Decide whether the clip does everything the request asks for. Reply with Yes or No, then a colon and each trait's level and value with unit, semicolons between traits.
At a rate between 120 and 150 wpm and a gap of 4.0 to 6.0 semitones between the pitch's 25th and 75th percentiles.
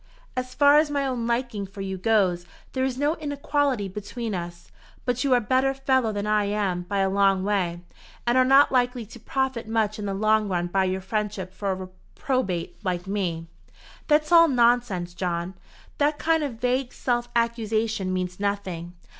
No: average, 185 wpm; average, 5.1 semitones